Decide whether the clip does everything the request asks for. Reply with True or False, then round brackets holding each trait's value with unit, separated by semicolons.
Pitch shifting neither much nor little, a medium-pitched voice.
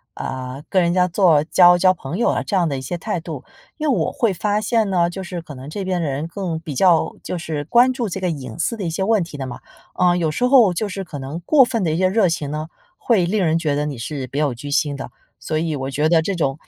True (4.5 semitones; 170 Hz)